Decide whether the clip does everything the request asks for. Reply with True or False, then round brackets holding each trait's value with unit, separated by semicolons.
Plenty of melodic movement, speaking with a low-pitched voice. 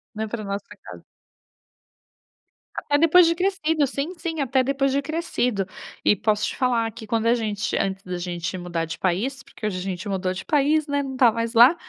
False (6.4 semitones; 235 Hz)